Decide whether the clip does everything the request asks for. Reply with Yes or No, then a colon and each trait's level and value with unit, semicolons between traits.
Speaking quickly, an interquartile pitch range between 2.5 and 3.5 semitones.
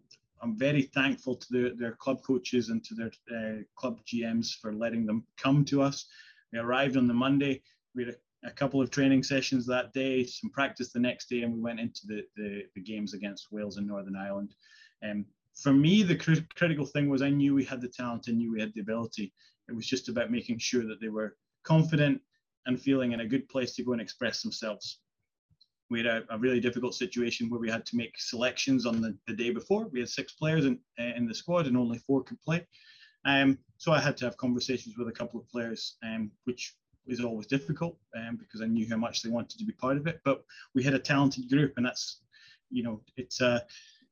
Yes: fast, 230 wpm; average, 3.1 semitones